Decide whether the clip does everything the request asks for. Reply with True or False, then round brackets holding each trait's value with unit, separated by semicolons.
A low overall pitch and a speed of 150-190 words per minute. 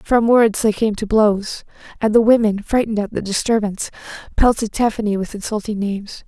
False (215 Hz; 170 wpm)